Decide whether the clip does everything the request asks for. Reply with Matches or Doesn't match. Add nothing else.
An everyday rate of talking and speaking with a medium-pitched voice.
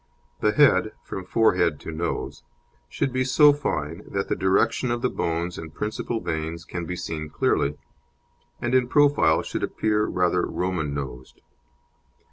Doesn't match